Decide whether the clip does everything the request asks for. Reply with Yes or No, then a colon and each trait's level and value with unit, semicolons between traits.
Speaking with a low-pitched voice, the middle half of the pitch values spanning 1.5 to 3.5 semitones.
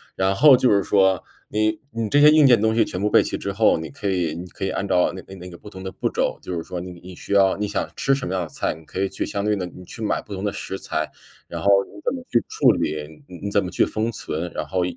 Yes: very low, 95 Hz; average, 3.0 semitones